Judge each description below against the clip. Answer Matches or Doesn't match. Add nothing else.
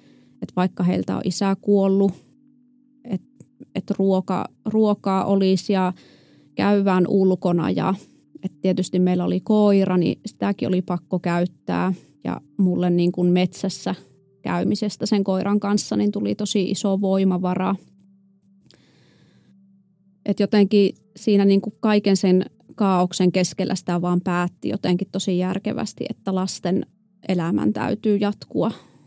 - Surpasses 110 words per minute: Matches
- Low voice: Doesn't match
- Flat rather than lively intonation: Matches